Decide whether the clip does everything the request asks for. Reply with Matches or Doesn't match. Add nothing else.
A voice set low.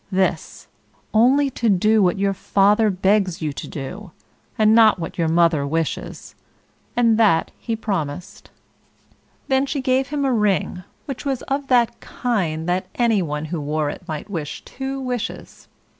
Doesn't match